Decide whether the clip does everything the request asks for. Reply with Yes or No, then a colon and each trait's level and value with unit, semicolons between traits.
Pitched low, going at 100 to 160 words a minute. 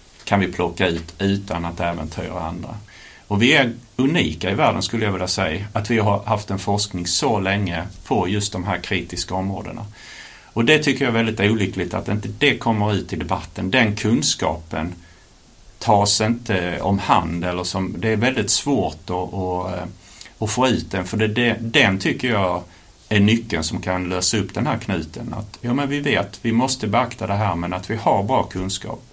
No: low, 100 Hz; average, 190 wpm